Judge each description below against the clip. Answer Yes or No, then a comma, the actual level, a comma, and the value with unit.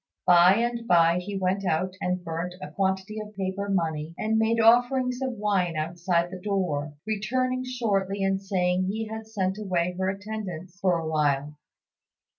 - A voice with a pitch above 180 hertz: Yes, high, 190 Hz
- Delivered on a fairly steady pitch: No, average, 3.6 semitones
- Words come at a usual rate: Yes, average, 165 wpm